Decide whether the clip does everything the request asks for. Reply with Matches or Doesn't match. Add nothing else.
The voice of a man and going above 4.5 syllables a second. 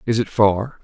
Doesn't match